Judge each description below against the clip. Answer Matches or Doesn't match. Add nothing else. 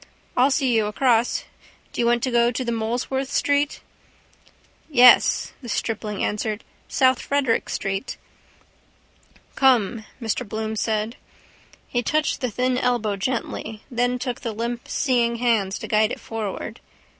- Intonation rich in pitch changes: Doesn't match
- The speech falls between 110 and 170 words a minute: Matches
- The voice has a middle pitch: Doesn't match